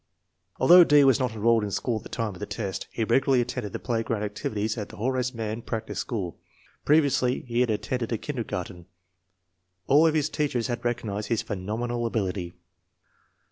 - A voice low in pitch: Yes, low, 115 Hz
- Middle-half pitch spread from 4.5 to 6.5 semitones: No, average, 3.1 semitones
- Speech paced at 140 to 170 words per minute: No, average, 180 wpm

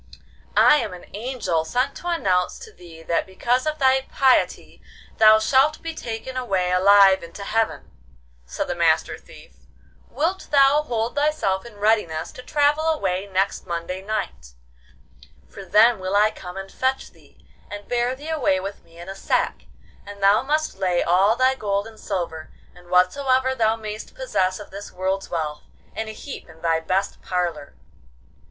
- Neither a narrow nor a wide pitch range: No, wide, 6.0 semitones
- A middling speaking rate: Yes, average, 170 wpm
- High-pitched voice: Yes, high, 205 Hz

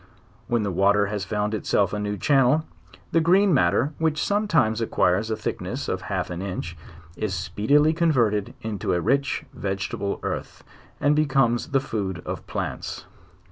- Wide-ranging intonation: Yes, wide, 6.4 semitones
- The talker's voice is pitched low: Yes, low, 110 Hz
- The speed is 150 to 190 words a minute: Yes, average, 155 wpm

